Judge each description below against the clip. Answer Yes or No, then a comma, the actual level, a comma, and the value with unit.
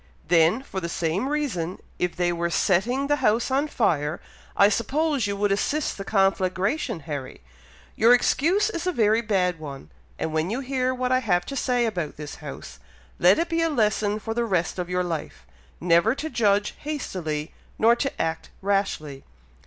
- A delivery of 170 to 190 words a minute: Yes, average, 180 wpm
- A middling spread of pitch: No, wide, 6.7 semitones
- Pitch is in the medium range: No, high, 200 Hz